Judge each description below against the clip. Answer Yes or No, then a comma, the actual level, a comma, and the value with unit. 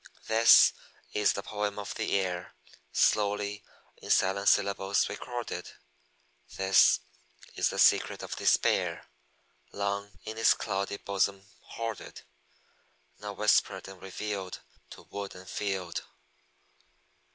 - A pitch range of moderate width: No, narrow, 1.3 semitones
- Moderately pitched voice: No, low, 100 Hz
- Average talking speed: No, slow, 110 wpm